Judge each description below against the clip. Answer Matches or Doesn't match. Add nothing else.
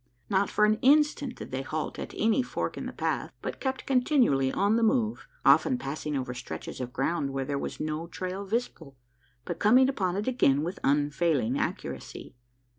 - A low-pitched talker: Doesn't match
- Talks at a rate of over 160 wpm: Matches